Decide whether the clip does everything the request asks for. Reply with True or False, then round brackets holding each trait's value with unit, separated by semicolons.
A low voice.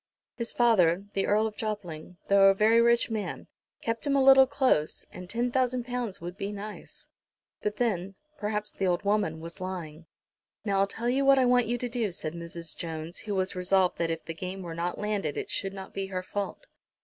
False (200 Hz)